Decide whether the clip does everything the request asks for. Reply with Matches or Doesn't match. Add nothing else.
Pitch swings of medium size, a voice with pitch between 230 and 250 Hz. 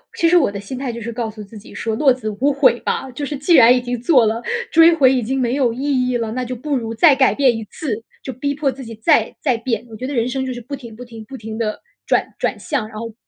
Matches